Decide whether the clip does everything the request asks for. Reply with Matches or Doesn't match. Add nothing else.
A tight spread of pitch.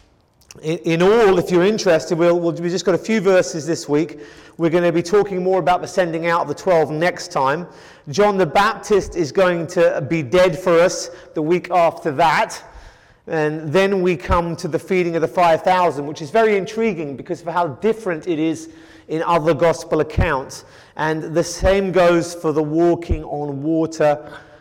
Matches